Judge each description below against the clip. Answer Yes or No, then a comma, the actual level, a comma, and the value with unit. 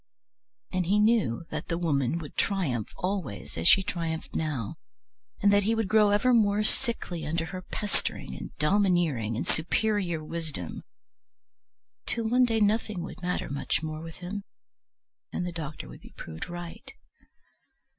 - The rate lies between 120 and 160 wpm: Yes, average, 155 wpm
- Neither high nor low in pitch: Yes, medium, 175 Hz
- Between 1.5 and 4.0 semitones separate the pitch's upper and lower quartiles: No, average, 4.9 semitones